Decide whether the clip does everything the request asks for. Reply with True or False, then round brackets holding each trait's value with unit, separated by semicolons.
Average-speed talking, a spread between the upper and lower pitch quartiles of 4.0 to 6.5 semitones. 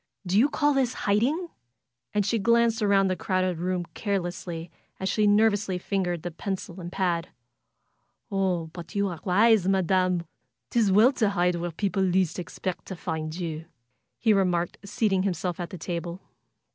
False (160 wpm; 2.9 semitones)